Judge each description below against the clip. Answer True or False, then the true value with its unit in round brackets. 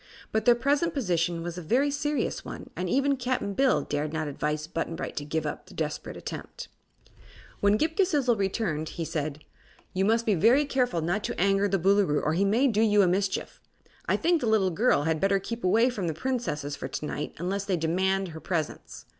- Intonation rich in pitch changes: True (6.5 semitones)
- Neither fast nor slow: False (210 wpm)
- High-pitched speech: True (195 Hz)